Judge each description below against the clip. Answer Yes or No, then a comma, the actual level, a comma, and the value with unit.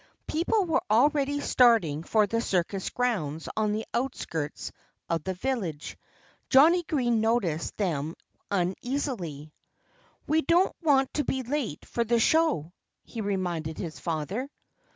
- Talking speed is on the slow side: Yes, slow, 130 wpm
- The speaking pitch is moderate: No, high, 220 Hz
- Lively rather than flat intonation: Yes, wide, 8.1 semitones